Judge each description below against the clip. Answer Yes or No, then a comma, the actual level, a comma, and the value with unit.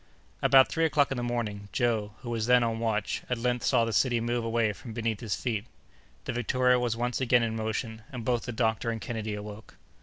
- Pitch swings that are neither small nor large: No, narrow, 1.8 semitones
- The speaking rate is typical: No, fast, 220 wpm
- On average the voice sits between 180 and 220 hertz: No, low, 115 Hz